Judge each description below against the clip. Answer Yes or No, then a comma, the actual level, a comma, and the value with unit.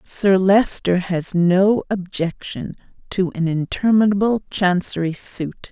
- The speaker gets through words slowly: Yes, slow, 105 wpm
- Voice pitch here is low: No, medium, 185 Hz